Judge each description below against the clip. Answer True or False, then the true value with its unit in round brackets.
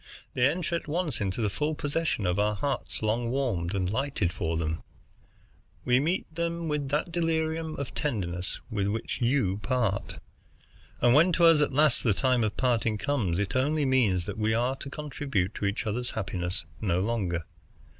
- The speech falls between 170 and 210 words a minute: True (175 wpm)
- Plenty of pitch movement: True (6.7 semitones)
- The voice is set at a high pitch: False (120 Hz)